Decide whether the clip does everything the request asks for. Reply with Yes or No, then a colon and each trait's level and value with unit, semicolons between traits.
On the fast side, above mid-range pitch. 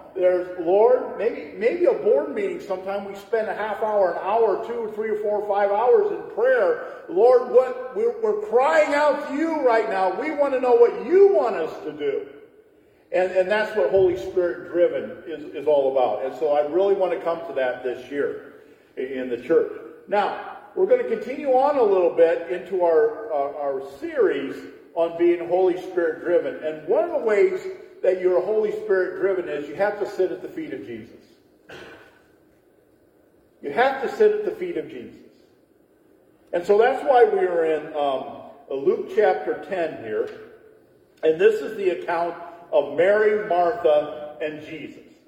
No: average, 185 wpm; high, 225 Hz